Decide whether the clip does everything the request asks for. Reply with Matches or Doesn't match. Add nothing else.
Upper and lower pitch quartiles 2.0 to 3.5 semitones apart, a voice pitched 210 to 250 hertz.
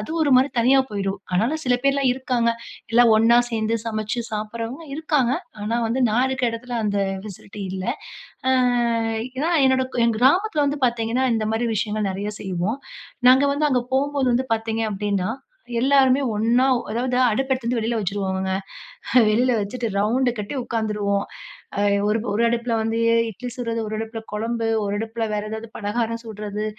Matches